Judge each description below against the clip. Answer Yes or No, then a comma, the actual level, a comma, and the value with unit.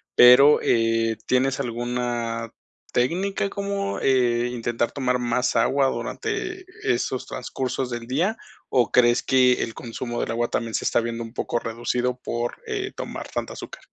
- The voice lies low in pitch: Yes, low, 125 Hz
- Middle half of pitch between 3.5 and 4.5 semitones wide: No, narrow, 2.4 semitones